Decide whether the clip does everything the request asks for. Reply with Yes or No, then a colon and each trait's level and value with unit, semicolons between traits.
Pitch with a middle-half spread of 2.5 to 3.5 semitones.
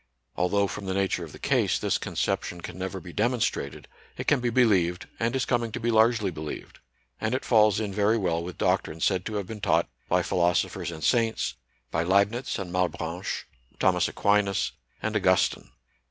No: average, 3.9 semitones